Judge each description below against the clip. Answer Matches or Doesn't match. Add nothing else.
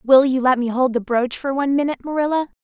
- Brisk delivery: Matches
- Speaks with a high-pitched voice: Matches